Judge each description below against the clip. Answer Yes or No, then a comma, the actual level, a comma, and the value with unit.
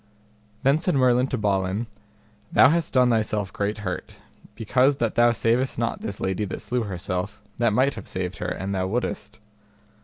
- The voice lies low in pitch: Yes, low, 110 Hz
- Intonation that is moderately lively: Yes, average, 4.2 semitones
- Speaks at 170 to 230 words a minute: Yes, average, 175 wpm